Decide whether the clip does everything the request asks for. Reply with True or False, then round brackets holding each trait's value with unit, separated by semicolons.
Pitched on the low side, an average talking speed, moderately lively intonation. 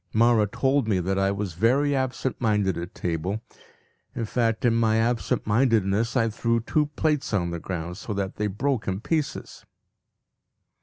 True (110 Hz; 165 wpm; 3.9 semitones)